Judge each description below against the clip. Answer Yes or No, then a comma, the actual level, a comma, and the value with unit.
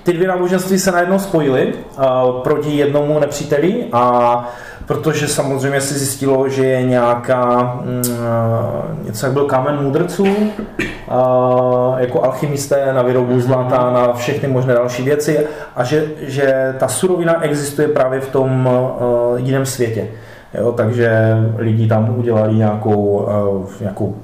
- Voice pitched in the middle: No, low, 130 Hz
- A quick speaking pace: No, average, 135 wpm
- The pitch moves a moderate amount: Yes, average, 3.3 semitones